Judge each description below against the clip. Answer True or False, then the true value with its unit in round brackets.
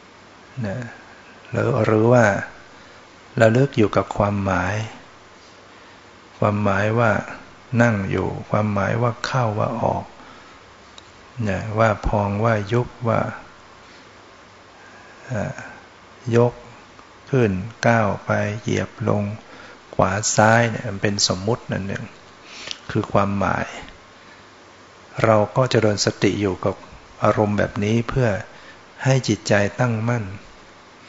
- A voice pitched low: True (110 Hz)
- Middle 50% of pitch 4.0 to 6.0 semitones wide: False (2.6 semitones)